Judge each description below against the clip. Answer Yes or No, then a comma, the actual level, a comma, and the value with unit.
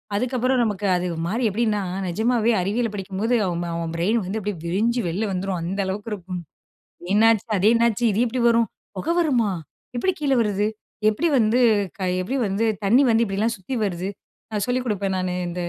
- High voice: Yes, high, 210 Hz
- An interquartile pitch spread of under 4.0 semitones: Yes, average, 3.6 semitones